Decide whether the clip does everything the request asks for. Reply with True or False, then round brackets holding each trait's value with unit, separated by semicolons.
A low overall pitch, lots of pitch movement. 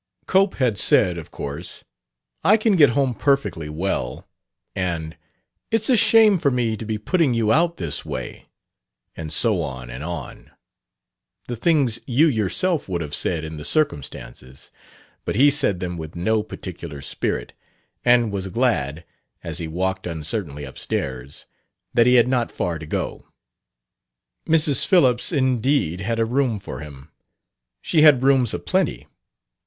True (105 Hz; 8.8 semitones)